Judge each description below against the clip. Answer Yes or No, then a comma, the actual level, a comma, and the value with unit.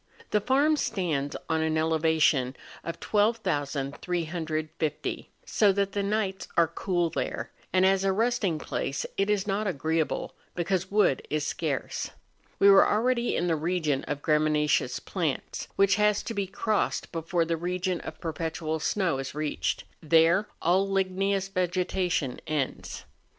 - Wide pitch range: No, average, 3.8 semitones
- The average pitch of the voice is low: No, medium, 175 Hz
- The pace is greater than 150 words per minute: No, average, 140 wpm